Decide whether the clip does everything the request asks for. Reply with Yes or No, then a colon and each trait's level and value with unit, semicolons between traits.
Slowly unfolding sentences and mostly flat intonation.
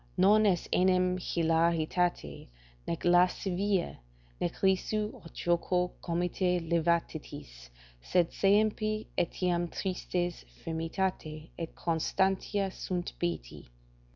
Yes: slow, 90 wpm; narrow, 2.2 semitones